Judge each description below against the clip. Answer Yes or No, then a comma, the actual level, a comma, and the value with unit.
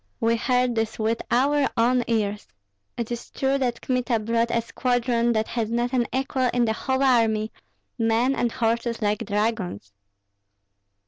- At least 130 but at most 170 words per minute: Yes, average, 155 wpm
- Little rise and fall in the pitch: Yes, narrow, 2.0 semitones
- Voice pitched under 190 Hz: No, high, 235 Hz